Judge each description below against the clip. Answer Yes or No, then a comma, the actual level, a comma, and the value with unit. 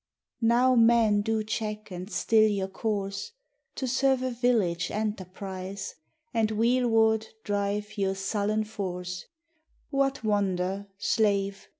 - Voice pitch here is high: Yes, high, 210 Hz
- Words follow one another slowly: Yes, slow, 110 wpm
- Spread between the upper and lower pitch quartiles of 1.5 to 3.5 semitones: Yes, narrow, 2.5 semitones